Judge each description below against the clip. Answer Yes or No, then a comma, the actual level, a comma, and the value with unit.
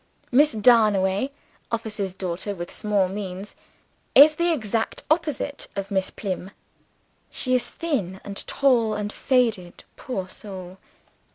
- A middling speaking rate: No, slow, 120 wpm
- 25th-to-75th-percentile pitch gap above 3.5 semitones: Yes, average, 4.9 semitones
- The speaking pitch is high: Yes, high, 210 Hz